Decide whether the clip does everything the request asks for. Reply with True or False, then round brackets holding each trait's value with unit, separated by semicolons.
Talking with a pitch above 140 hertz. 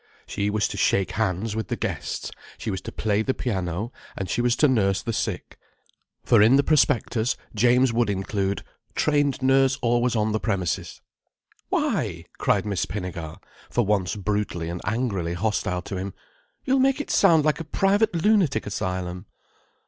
False (110 Hz)